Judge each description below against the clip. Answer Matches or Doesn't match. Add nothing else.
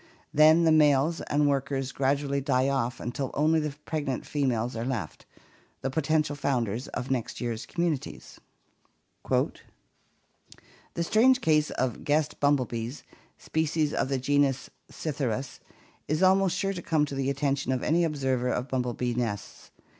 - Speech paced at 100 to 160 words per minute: Matches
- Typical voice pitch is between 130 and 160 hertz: Matches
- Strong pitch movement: Doesn't match